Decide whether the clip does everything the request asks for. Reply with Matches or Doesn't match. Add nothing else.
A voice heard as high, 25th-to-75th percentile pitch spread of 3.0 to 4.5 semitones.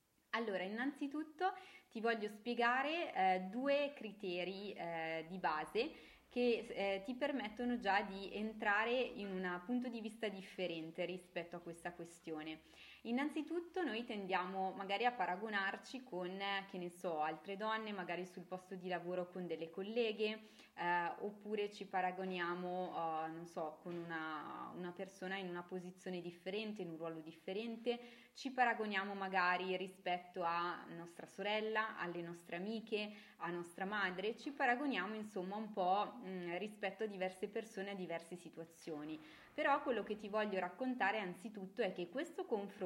Matches